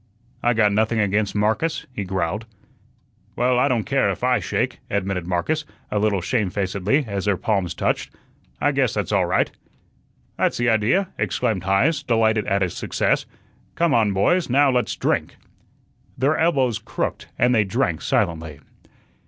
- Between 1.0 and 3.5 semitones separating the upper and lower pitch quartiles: No, average, 4.4 semitones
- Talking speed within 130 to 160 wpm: Yes, average, 155 wpm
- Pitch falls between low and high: No, low, 110 Hz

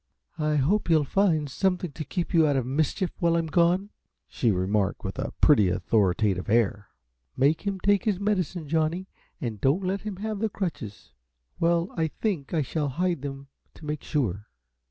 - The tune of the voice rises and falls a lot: Yes, wide, 5.7 semitones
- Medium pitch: Yes, medium, 155 Hz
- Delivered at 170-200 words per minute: Yes, average, 175 wpm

